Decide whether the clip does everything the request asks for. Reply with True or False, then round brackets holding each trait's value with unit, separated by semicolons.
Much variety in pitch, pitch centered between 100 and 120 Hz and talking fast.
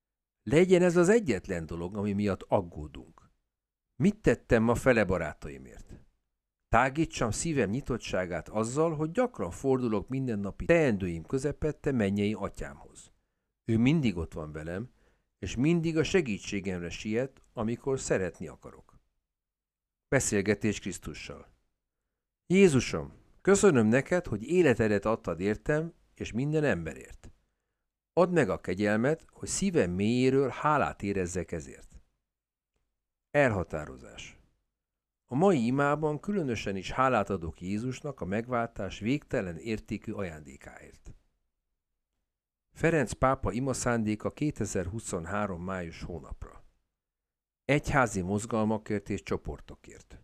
False (6.4 semitones; 110 Hz; 105 wpm)